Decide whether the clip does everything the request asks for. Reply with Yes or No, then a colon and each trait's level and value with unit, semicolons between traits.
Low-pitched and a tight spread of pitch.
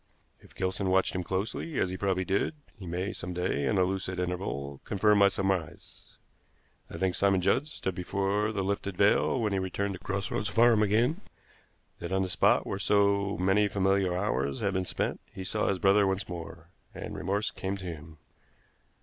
Yes: very low, 95 Hz; narrow, 1.8 semitones